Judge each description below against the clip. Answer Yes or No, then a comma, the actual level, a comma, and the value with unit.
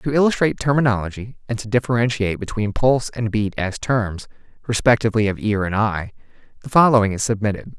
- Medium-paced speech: Yes, average, 160 wpm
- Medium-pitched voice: No, low, 115 Hz